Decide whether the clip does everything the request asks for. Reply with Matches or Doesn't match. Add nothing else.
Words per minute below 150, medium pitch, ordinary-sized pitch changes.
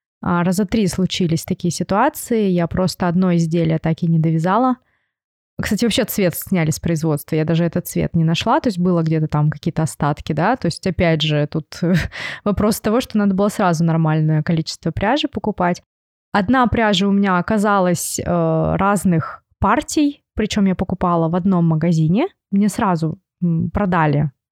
Doesn't match